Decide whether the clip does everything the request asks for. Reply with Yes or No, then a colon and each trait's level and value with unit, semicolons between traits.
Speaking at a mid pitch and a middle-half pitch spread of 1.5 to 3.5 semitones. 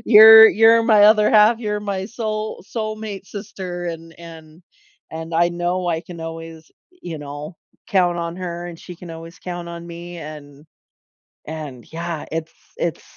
No: medium, 175 Hz; average, 4.2 semitones